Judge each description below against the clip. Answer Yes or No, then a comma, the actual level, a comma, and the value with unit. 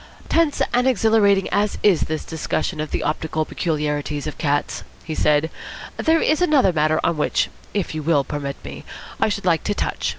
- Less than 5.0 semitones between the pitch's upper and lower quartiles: No, wide, 5.5 semitones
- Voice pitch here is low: No, medium, 160 Hz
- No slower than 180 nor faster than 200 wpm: Yes, average, 185 wpm